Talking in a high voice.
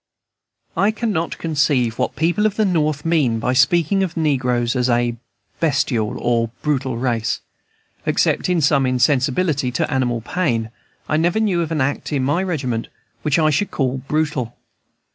No: medium, 140 Hz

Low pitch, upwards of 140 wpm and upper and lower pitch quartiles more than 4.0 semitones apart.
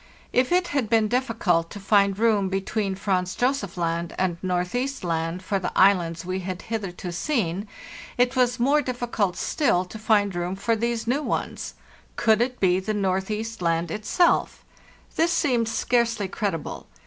No: high, 205 Hz; average, 160 wpm; average, 4.6 semitones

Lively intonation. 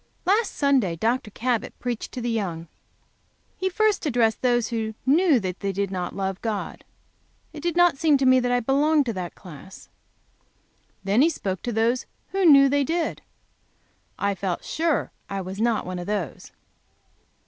Yes: wide, 6.5 semitones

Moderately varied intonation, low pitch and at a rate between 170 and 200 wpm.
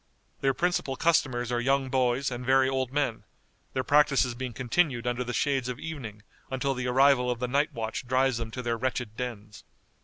No: narrow, 1.9 semitones; low, 130 Hz; average, 190 wpm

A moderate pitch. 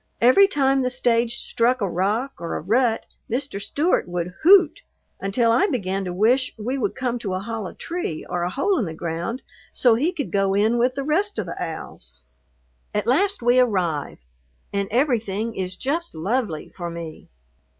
No: high, 230 Hz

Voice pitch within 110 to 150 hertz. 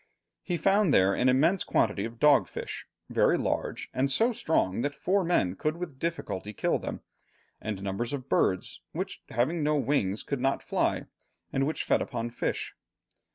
Yes: low, 135 Hz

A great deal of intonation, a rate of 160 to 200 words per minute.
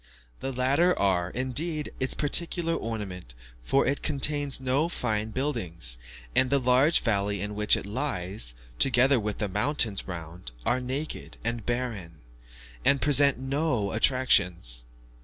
No: wide, 5.7 semitones; slow, 135 wpm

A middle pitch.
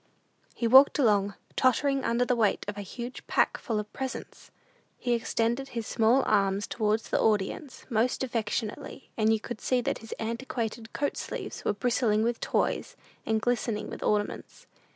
No: high, 230 Hz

